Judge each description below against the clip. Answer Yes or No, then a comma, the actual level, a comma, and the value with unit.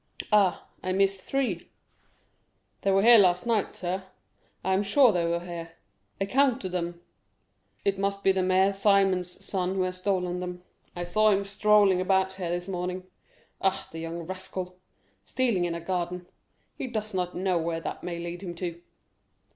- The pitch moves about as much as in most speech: No, narrow, 2.0 semitones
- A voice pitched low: No, medium, 185 Hz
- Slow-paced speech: No, average, 165 wpm